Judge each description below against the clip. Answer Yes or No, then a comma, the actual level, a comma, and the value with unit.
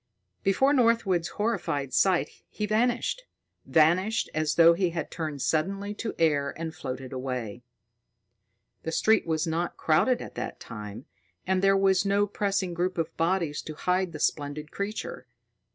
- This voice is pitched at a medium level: Yes, medium, 170 Hz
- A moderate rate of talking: Yes, average, 150 wpm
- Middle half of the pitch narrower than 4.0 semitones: No, average, 4.4 semitones